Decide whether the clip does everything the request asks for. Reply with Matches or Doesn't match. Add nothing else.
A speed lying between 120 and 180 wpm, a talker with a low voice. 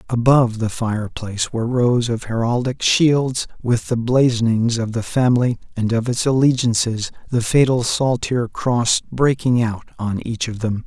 Matches